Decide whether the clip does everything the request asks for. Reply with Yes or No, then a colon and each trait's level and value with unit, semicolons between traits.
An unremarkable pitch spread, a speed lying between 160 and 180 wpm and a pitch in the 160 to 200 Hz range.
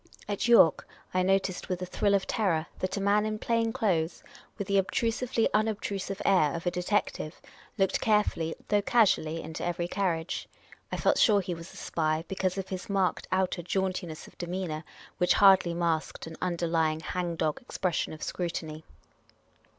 Yes: average, 3.2 semitones; average, 175 wpm; medium, 185 Hz